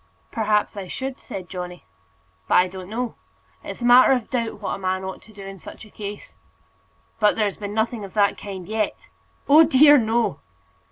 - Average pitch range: Yes, average, 3.4 semitones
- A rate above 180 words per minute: Yes, average, 190 wpm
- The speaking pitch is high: Yes, high, 210 Hz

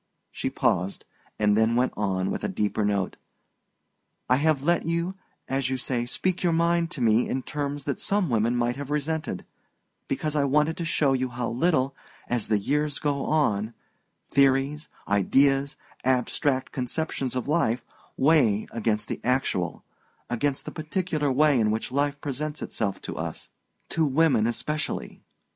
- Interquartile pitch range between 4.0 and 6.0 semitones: Yes, average, 4.4 semitones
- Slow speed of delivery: No, average, 155 wpm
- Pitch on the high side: No, low, 135 Hz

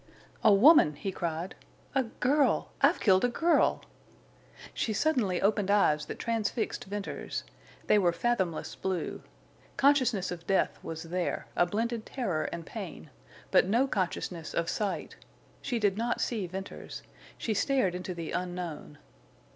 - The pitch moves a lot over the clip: No, average, 4.9 semitones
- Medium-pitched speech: No, high, 195 Hz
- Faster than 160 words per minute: No, average, 140 wpm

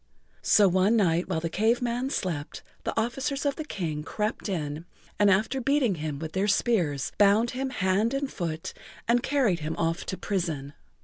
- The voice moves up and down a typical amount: No, wide, 6.5 semitones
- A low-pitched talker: No, high, 200 Hz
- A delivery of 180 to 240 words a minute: Yes, average, 185 wpm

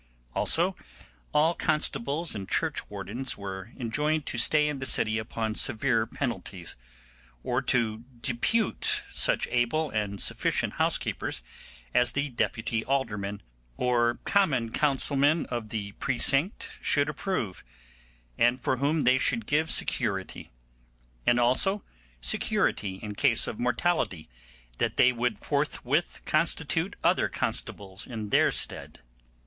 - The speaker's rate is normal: No, slow, 120 wpm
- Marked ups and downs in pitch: No, average, 4.8 semitones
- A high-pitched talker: No, low, 120 Hz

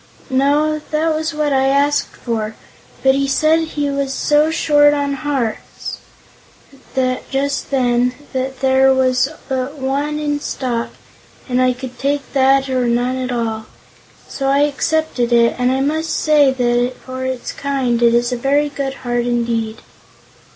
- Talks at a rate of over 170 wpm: No, average, 155 wpm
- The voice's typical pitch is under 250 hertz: No, very high, 265 Hz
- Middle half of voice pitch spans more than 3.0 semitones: No, narrow, 2.6 semitones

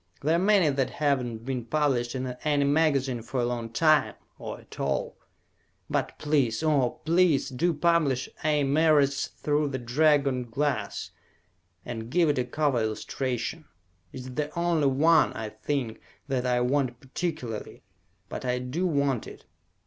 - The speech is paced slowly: No, average, 155 wpm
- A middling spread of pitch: Yes, average, 3.6 semitones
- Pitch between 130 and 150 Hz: Yes, medium, 140 Hz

